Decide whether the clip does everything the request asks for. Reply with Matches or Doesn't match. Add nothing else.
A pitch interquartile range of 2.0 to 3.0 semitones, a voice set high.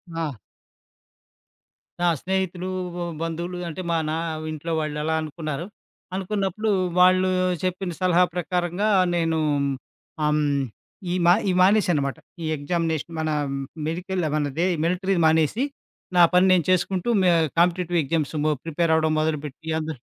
Doesn't match